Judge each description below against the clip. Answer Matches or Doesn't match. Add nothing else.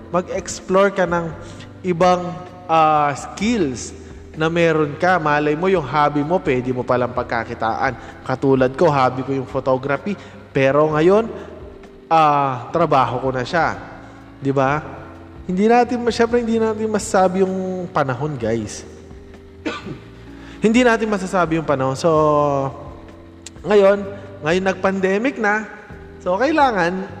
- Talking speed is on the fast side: Doesn't match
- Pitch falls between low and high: Matches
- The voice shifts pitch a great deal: Matches